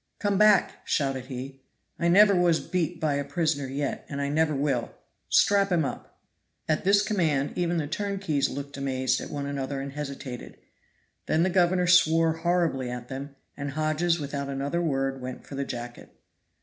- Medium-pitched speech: Yes, medium, 145 Hz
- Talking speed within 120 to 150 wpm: No, average, 175 wpm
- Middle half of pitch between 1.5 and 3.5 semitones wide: No, average, 4.2 semitones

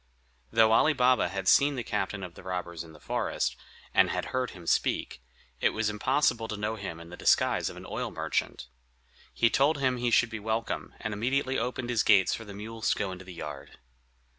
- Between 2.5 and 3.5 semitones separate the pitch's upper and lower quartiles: No, average, 4.7 semitones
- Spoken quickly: Yes, fast, 215 wpm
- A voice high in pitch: No, low, 110 Hz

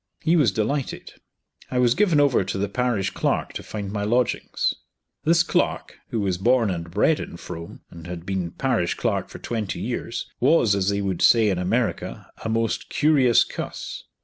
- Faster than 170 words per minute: Yes, average, 180 wpm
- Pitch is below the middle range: Yes, low, 110 Hz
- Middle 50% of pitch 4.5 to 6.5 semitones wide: Yes, average, 4.8 semitones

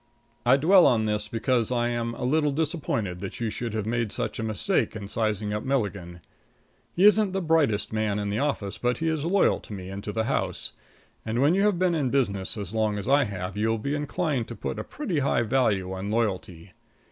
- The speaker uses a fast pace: Yes, fast, 225 wpm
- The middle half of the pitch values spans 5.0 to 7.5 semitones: Yes, average, 5.3 semitones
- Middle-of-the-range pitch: No, low, 115 Hz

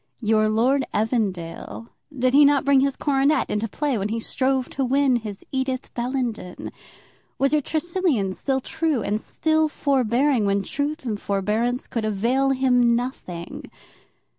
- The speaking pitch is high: Yes, very high, 255 Hz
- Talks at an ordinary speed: Yes, average, 145 wpm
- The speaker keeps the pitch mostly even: No, average, 4.2 semitones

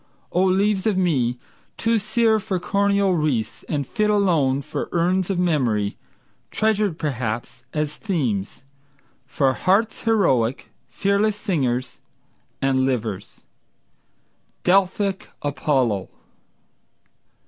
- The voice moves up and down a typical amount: No, wide, 7.3 semitones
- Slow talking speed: Yes, slow, 100 wpm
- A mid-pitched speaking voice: Yes, medium, 170 Hz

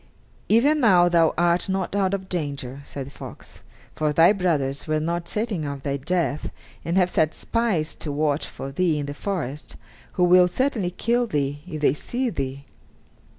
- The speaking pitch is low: No, medium, 170 Hz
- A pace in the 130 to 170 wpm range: No, average, 180 wpm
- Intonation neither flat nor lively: Yes, average, 4.7 semitones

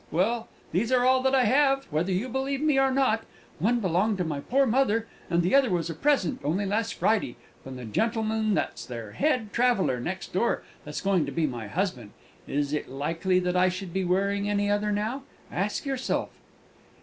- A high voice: Yes, high, 200 Hz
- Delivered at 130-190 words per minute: No, average, 200 wpm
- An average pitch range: No, wide, 6.2 semitones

